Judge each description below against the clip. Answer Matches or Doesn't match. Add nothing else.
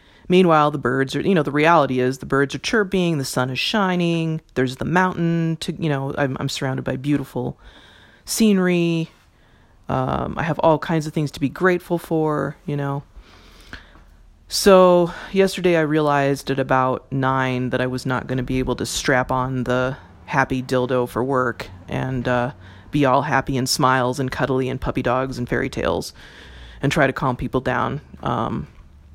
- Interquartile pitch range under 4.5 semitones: Matches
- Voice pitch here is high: Doesn't match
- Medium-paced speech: Matches